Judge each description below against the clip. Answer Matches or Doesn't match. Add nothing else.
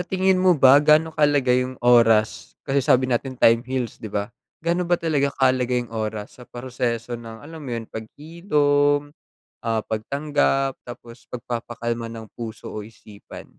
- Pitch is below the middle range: Matches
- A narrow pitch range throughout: Doesn't match